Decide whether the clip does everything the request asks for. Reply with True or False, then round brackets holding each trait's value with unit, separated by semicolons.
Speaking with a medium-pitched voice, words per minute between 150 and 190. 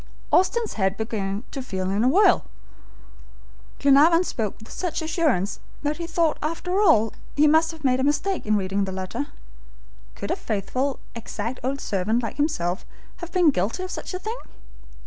False (275 Hz; 170 wpm)